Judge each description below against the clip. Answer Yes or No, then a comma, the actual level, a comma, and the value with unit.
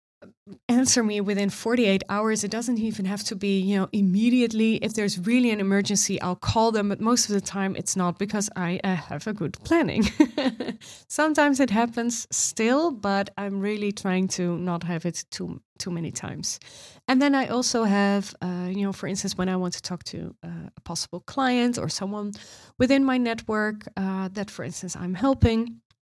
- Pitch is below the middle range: No, high, 205 Hz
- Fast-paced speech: No, average, 195 wpm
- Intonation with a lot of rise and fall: No, average, 3.7 semitones